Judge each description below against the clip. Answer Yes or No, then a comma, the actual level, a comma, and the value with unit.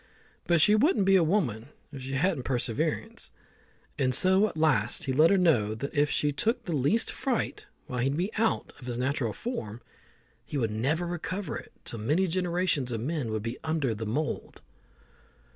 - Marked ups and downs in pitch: Yes, wide, 6.7 semitones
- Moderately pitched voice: Yes, medium, 145 Hz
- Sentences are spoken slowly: No, average, 185 wpm